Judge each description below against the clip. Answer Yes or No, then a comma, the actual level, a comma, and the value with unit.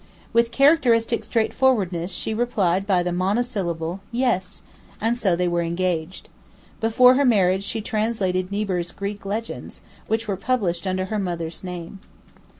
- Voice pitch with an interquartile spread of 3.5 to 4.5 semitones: Yes, average, 4.1 semitones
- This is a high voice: Yes, high, 200 Hz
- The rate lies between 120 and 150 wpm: Yes, average, 140 wpm